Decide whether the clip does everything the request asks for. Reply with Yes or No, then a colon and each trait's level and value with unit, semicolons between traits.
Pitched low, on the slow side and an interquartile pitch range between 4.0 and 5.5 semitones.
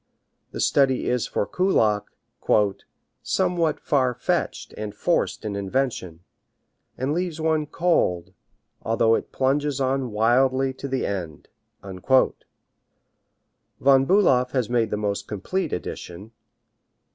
Yes: low, 130 Hz; slow, 110 wpm; average, 5.1 semitones